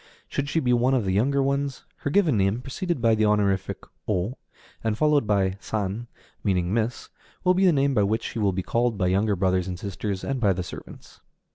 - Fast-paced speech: Yes, fast, 215 wpm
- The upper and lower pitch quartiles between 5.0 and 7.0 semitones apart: Yes, wide, 5.6 semitones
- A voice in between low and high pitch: No, low, 110 Hz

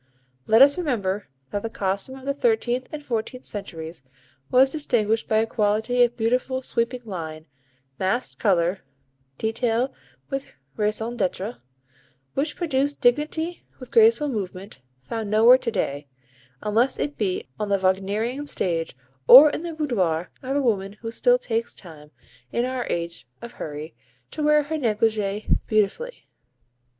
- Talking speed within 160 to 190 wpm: No, average, 145 wpm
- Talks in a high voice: Yes, high, 225 Hz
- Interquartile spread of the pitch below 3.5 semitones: No, average, 5.2 semitones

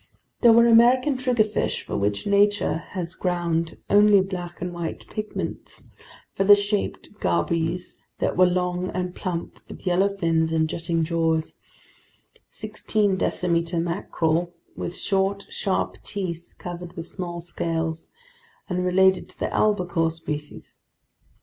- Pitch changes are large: No, average, 3.1 semitones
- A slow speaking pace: Yes, slow, 125 wpm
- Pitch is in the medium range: Yes, medium, 180 Hz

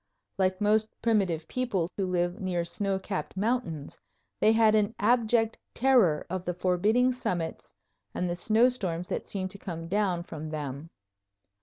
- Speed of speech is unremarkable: Yes, average, 150 wpm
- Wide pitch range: No, average, 4.0 semitones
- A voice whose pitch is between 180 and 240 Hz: Yes, high, 190 Hz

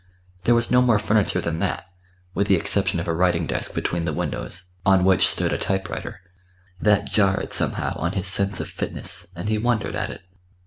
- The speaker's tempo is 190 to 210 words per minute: Yes, average, 195 wpm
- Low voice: Yes, very low, 95 Hz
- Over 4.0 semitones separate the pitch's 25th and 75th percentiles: No, average, 3.3 semitones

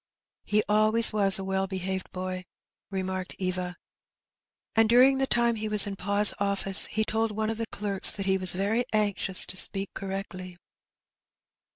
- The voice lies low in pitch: No, high, 200 Hz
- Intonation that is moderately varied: No, narrow, 2.2 semitones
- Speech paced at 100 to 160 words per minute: No, average, 170 wpm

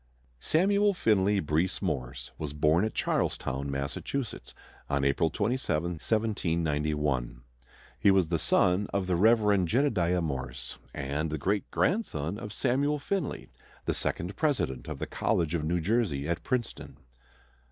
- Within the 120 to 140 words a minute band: Yes, slow, 135 wpm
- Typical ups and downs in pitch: No, wide, 6.8 semitones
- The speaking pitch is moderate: No, very low, 85 Hz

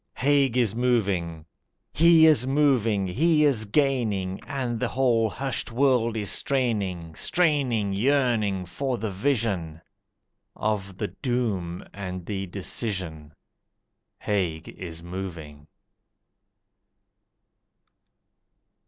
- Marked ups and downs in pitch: Yes, wide, 6.0 semitones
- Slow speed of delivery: Yes, slow, 95 wpm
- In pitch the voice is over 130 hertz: No, low, 110 Hz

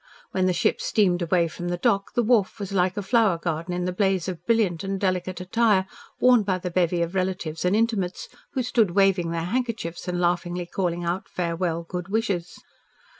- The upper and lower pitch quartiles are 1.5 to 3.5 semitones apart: Yes, narrow, 2.4 semitones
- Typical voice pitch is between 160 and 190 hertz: Yes, medium, 185 Hz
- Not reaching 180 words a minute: No, average, 195 wpm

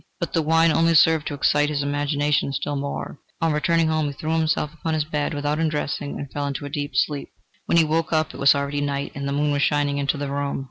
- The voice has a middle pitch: Yes, medium, 145 Hz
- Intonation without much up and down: Yes, narrow, 1.8 semitones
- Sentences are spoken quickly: Yes, fast, 245 wpm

